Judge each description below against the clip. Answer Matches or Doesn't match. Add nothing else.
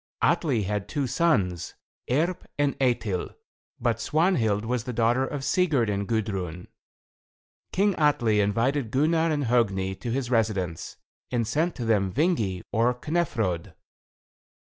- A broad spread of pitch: Matches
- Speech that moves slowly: Matches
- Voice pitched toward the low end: Matches